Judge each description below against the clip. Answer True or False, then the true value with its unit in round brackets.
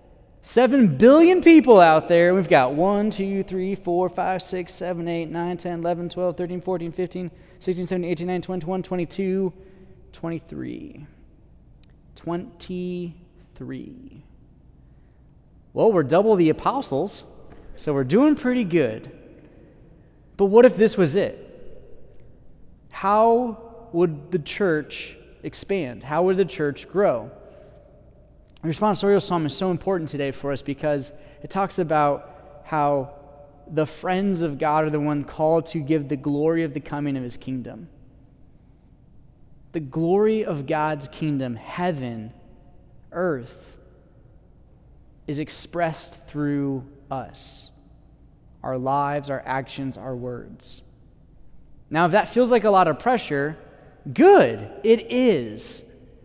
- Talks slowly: True (125 wpm)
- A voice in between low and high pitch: True (170 Hz)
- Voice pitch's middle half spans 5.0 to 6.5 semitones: False (4.6 semitones)